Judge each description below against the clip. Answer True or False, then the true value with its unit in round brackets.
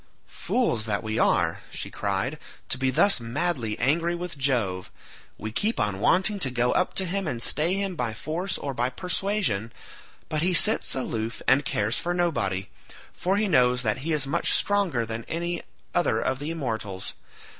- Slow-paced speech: False (175 wpm)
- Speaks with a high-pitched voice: False (135 Hz)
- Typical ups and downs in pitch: False (7.5 semitones)